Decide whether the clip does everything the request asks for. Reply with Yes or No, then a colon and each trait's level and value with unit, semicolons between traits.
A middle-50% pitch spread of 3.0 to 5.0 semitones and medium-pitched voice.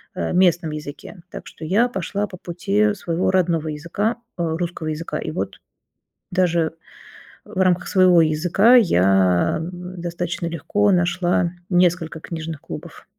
No: narrow, 2.5 semitones; medium, 175 Hz